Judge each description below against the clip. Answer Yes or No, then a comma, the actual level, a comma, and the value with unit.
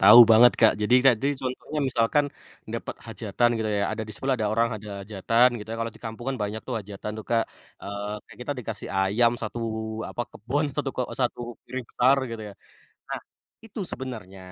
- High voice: No, low, 115 Hz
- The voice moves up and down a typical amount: Yes, average, 3.0 semitones